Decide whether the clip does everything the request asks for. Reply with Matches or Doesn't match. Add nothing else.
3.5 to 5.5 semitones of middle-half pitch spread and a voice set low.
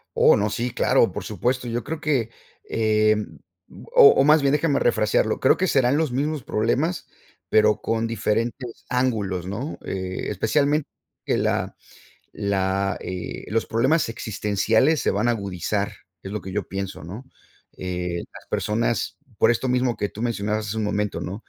Matches